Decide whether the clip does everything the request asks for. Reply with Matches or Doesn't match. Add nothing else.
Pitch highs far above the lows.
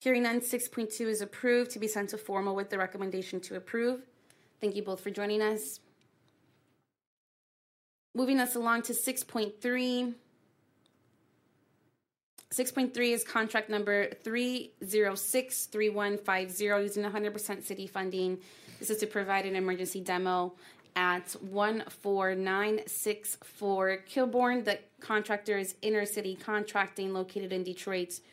Doesn't match